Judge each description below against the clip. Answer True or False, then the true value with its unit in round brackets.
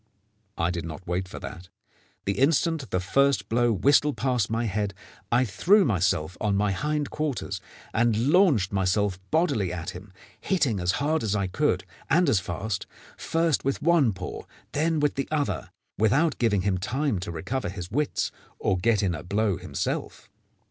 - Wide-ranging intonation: True (7.0 semitones)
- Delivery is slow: False (175 wpm)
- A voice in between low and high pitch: False (110 Hz)